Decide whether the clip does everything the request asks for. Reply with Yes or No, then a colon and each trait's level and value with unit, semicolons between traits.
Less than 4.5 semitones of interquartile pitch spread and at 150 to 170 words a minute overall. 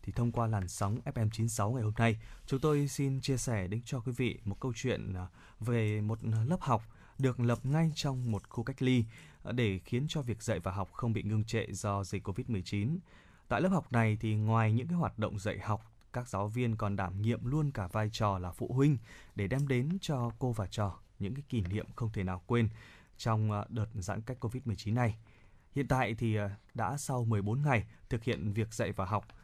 No: average, 3.4 semitones; average, 215 wpm